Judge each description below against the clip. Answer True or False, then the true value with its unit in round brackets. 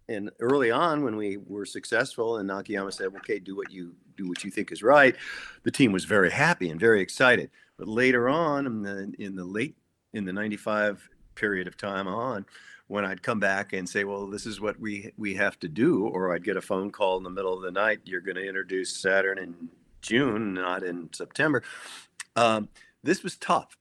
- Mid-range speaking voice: False (100 Hz)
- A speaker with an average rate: False (210 wpm)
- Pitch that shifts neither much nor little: False (2.2 semitones)